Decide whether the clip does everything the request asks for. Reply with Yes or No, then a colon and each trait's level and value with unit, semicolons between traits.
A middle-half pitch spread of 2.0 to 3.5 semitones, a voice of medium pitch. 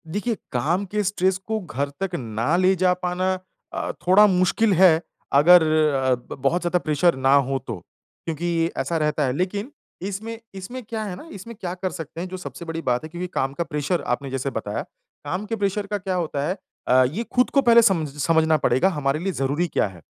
No: average, 4.8 semitones; medium, 175 Hz